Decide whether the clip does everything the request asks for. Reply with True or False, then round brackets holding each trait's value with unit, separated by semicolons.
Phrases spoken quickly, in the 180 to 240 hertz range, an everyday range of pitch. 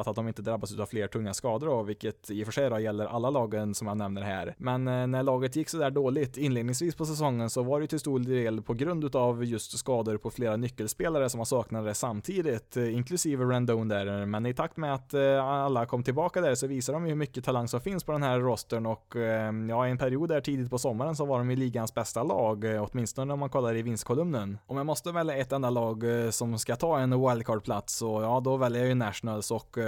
False (225 wpm; 120 Hz; 3.4 semitones)